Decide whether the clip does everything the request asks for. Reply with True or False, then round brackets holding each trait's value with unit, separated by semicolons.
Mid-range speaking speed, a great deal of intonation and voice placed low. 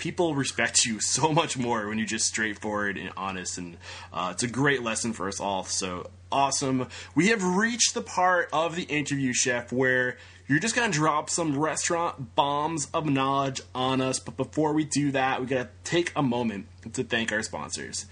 True (190 wpm; 6.3 semitones; 130 Hz)